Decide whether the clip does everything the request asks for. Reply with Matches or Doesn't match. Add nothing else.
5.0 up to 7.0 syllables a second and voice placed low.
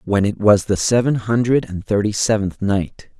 Doesn't match